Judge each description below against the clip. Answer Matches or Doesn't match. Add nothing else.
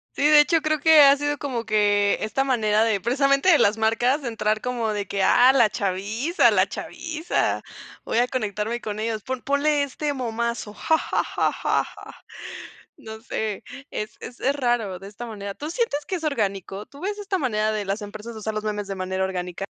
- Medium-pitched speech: Doesn't match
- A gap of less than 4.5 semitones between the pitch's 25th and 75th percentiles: Doesn't match